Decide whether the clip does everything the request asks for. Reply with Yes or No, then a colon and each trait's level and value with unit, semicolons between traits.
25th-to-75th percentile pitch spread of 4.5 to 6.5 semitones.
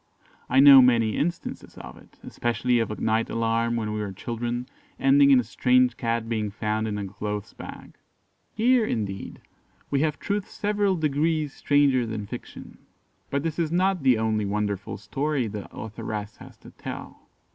Yes: average, 5.0 semitones